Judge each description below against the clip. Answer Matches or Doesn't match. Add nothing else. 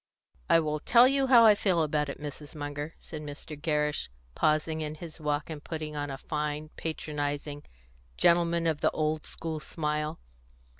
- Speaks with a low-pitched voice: Doesn't match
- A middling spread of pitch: Doesn't match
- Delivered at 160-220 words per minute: Matches